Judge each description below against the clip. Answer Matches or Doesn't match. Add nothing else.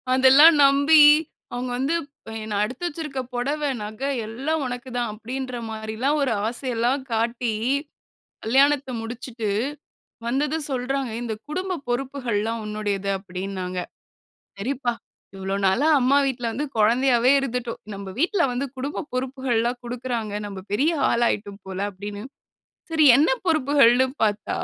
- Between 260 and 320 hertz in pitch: Doesn't match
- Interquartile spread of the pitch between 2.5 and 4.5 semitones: Matches